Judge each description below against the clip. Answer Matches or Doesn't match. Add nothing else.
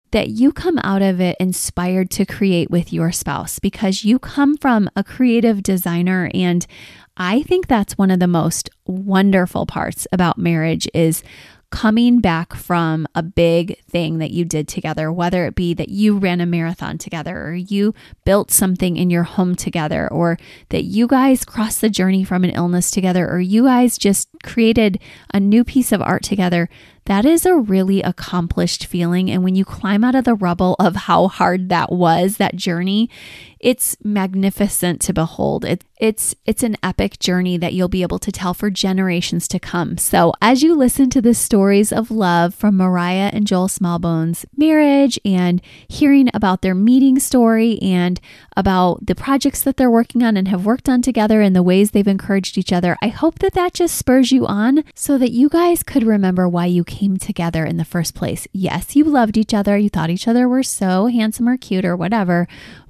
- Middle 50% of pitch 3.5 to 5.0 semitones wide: Matches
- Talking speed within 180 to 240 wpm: Matches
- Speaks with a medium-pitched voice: Doesn't match